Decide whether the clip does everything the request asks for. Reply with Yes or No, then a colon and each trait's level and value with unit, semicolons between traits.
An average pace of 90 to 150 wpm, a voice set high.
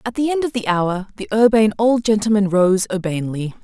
No: average, 200 wpm; high, 210 Hz